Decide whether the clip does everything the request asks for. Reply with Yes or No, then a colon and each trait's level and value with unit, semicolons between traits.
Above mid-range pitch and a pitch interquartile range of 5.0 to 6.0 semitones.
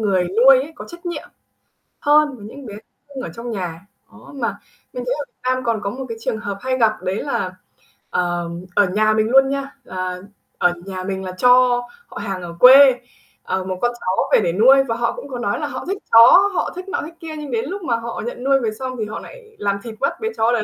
Yes: high, 235 Hz; average, 5.3 semitones